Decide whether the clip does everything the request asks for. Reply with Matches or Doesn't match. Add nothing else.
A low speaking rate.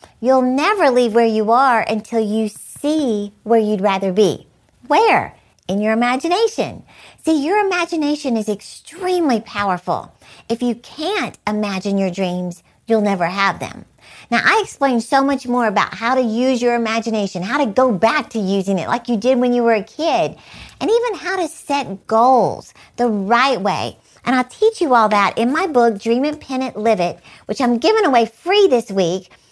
Doesn't match